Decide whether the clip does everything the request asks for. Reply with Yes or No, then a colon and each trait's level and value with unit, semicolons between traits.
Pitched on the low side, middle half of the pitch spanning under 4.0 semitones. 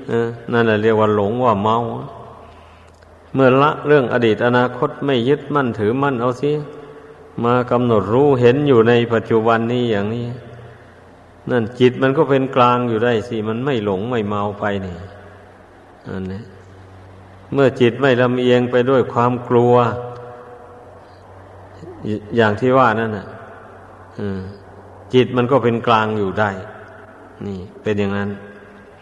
Yes: low, 115 Hz; average, 3.5 semitones